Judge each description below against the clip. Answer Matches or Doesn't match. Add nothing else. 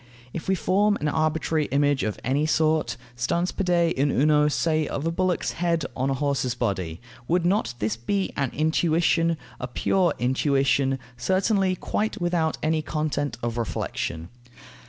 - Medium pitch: Matches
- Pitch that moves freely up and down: Doesn't match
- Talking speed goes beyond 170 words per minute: Doesn't match